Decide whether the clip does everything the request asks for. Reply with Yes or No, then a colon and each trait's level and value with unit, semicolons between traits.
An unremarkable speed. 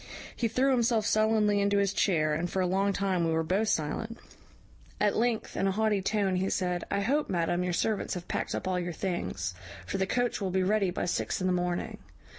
No: fast, 225 wpm